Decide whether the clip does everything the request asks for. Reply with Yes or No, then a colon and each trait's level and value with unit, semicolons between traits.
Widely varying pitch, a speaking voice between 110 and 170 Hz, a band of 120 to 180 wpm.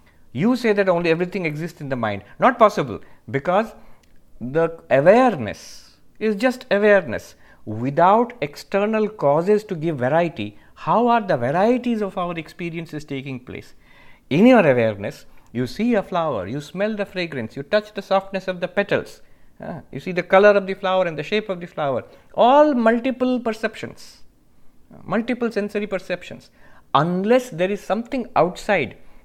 No: wide, 6.4 semitones; medium, 185 Hz; average, 155 wpm